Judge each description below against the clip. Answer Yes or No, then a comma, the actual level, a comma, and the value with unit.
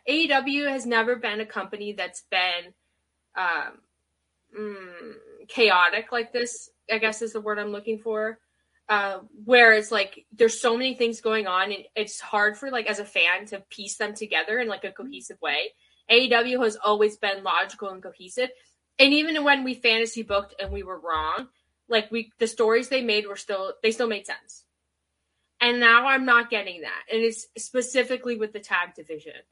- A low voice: No, high, 220 Hz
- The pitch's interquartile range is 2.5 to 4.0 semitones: Yes, average, 3.4 semitones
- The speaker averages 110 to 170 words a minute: No, average, 185 wpm